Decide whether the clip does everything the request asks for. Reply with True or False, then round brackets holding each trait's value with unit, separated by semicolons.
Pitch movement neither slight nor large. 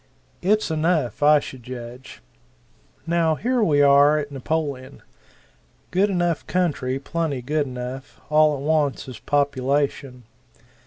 True (3.5 semitones)